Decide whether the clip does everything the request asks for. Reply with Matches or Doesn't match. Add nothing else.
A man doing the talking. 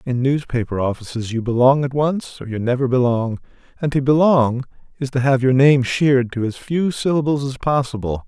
Matches